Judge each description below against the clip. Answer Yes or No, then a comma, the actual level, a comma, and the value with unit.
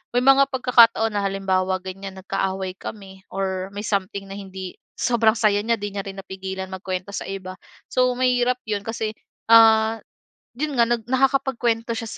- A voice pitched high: Yes, high, 205 Hz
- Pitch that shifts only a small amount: No, average, 3.5 semitones